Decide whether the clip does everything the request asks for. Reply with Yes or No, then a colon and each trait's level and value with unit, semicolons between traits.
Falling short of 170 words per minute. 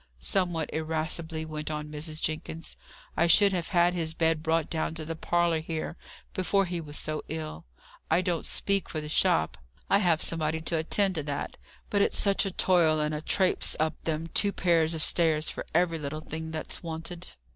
No: average, 190 wpm